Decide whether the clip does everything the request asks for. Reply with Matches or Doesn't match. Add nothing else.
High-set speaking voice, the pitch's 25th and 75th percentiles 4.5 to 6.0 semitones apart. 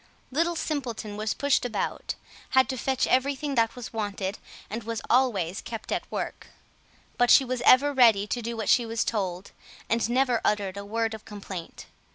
Doesn't match